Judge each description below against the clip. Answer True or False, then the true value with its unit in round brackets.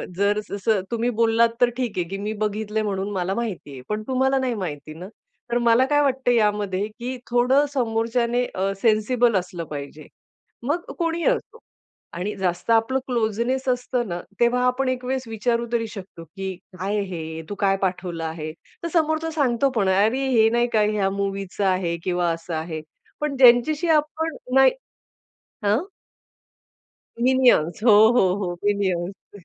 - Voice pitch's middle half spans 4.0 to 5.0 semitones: True (4.7 semitones)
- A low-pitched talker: False (220 Hz)